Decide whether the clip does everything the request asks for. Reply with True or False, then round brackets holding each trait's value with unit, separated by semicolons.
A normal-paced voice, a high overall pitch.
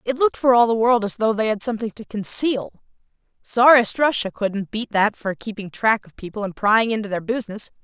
False (215 wpm; 220 Hz)